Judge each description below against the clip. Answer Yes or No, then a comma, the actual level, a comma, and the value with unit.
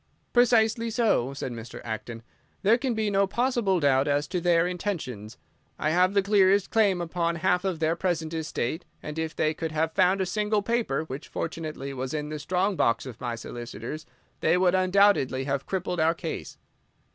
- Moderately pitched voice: Yes, medium, 170 Hz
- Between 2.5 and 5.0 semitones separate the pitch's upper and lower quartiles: No, wide, 5.4 semitones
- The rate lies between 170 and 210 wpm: Yes, average, 175 wpm